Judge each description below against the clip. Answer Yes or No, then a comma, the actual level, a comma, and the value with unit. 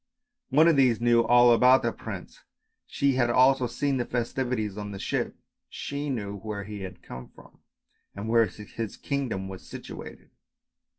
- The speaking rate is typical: Yes, average, 160 wpm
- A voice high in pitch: No, low, 120 Hz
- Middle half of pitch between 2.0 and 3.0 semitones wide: No, average, 3.8 semitones